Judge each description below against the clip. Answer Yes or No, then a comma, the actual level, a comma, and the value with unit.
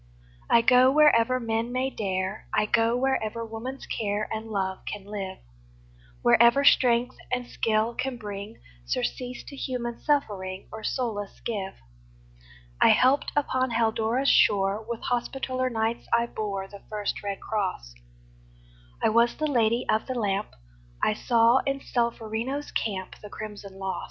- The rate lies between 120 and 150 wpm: Yes, average, 140 wpm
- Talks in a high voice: Yes, high, 225 Hz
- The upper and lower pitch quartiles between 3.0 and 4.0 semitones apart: Yes, average, 3.3 semitones